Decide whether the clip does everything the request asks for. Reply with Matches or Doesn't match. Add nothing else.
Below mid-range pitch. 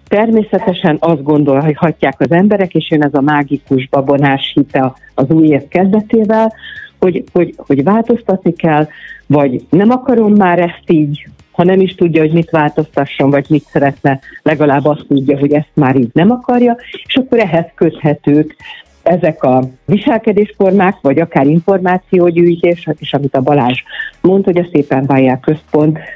Doesn't match